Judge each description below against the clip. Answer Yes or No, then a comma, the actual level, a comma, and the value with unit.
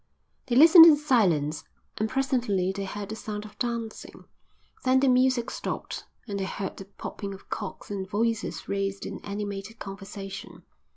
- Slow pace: No, average, 160 wpm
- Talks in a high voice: Yes, high, 210 Hz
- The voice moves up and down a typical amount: Yes, average, 3.7 semitones